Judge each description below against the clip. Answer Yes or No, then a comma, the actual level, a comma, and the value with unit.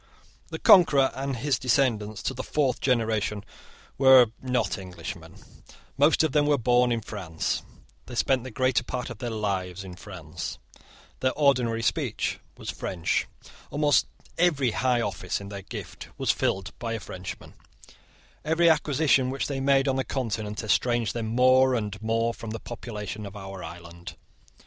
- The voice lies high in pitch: No, low, 120 Hz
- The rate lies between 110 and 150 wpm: No, average, 160 wpm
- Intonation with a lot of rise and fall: No, average, 4.2 semitones